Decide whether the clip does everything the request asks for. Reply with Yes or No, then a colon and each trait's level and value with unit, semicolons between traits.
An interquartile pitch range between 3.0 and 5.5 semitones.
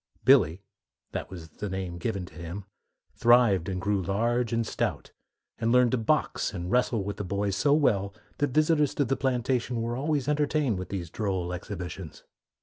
Yes: average, 5.0 semitones